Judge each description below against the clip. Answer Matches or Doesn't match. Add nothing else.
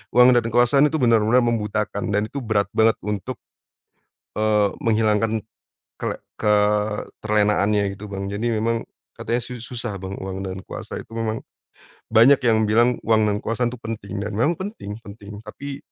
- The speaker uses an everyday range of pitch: Doesn't match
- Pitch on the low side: Matches